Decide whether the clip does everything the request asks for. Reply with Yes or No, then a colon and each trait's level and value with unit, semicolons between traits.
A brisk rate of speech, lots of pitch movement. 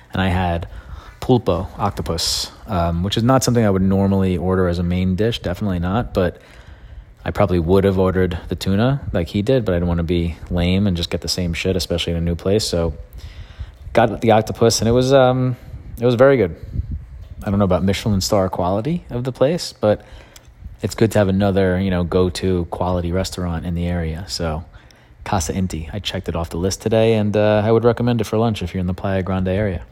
No: fast, 225 wpm; average, 3.3 semitones